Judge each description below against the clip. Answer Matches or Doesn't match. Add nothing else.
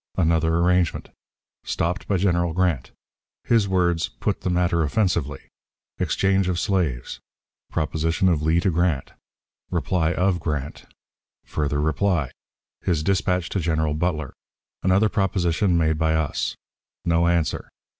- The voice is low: Matches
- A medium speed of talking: Doesn't match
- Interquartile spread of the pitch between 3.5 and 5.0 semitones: Doesn't match